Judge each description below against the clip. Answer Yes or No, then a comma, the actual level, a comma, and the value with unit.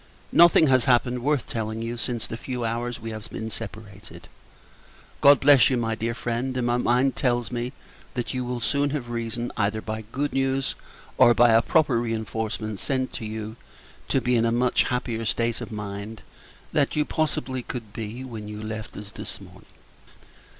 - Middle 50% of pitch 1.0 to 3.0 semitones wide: Yes, narrow, 2.5 semitones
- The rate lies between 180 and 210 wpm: Yes, average, 185 wpm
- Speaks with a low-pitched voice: Yes, low, 120 Hz